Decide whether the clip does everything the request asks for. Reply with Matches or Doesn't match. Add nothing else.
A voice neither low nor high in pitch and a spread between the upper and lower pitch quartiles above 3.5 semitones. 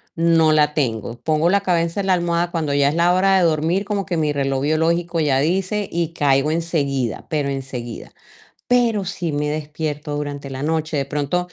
Doesn't match